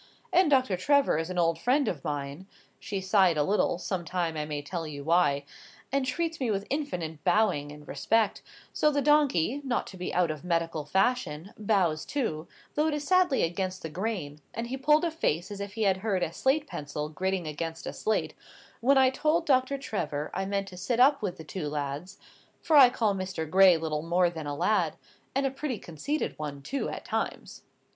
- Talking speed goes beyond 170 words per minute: Yes, fast, 205 wpm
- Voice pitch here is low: No, high, 190 Hz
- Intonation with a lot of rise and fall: Yes, wide, 8.3 semitones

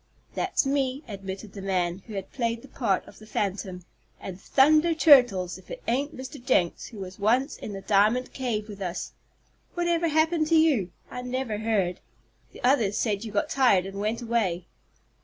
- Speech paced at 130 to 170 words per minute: No, average, 180 wpm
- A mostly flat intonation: No, wide, 5.4 semitones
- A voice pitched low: No, high, 225 Hz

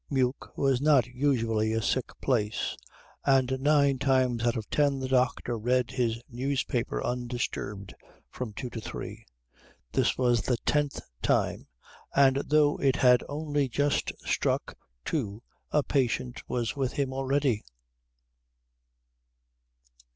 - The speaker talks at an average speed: No, slow, 125 wpm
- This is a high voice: No, low, 130 Hz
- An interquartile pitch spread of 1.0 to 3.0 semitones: Yes, narrow, 2.5 semitones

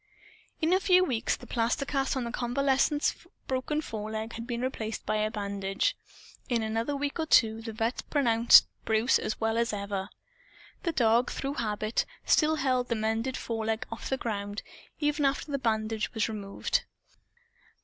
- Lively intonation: No, average, 3.7 semitones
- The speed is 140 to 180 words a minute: Yes, average, 165 wpm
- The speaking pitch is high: Yes, high, 230 Hz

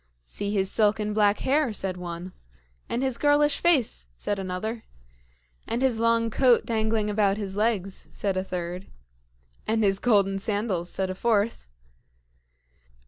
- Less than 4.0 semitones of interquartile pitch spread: Yes, average, 3.2 semitones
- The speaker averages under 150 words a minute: Yes, average, 140 wpm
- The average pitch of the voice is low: No, high, 210 Hz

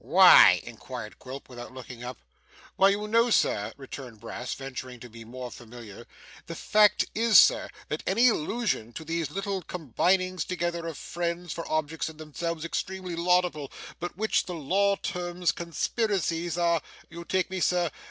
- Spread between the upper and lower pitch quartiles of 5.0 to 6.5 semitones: Yes, wide, 5.4 semitones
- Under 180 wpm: Yes, average, 160 wpm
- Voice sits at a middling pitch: Yes, medium, 170 Hz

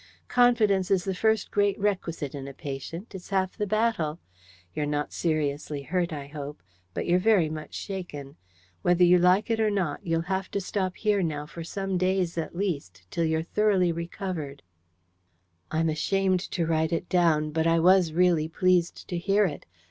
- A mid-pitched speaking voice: Yes, medium, 175 Hz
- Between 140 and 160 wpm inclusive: No, average, 180 wpm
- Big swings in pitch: No, average, 3.6 semitones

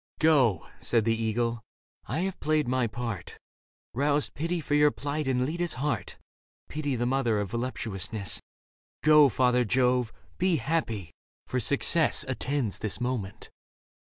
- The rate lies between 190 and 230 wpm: No, average, 145 wpm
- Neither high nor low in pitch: No, low, 125 Hz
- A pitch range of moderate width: Yes, average, 4.5 semitones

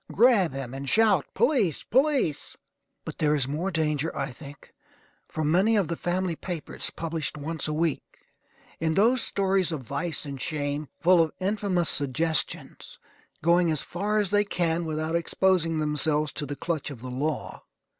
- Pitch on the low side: No, medium, 165 Hz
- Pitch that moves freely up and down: No, average, 4.0 semitones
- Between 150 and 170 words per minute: Yes, average, 165 wpm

